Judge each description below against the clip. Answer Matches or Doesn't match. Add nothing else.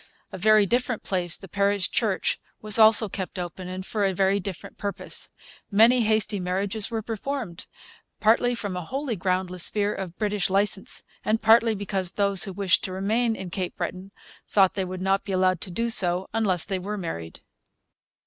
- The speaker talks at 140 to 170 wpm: Doesn't match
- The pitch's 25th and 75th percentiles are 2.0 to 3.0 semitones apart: Matches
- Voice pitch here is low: Doesn't match